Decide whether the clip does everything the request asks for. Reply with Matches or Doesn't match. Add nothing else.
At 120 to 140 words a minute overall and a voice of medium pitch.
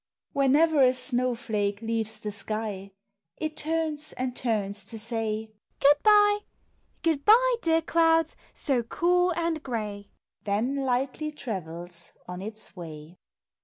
Doesn't match